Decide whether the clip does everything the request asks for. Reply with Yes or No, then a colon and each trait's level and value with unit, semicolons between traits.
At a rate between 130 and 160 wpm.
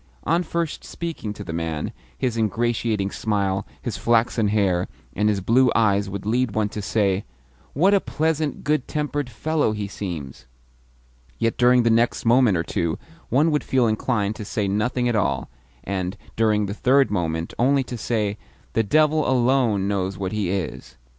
No: average, 170 wpm